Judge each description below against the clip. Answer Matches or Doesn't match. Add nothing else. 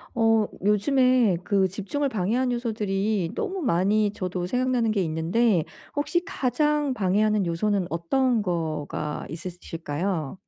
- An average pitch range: Doesn't match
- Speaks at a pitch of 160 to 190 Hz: Doesn't match